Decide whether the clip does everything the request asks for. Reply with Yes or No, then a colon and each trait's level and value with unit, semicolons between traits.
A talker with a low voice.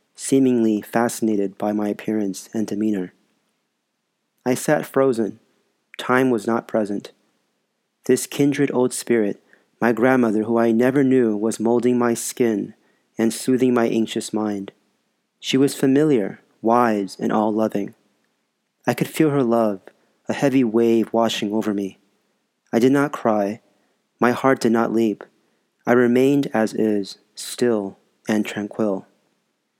Yes: low, 115 Hz